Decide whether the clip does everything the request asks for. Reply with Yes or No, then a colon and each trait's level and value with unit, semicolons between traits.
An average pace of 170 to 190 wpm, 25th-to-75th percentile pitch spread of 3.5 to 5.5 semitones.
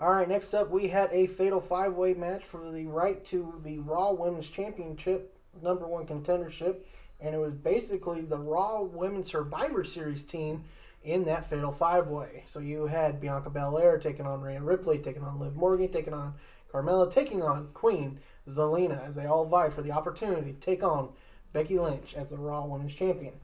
Yes: average, 185 wpm; average, 3.9 semitones